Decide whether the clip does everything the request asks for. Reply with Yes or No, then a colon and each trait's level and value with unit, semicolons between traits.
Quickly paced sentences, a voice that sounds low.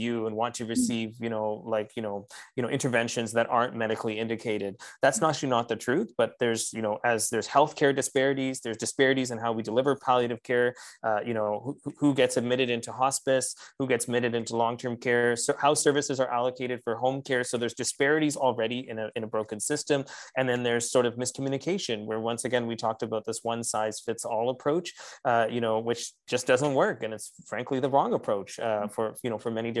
Yes: fast, 215 wpm; low, 120 Hz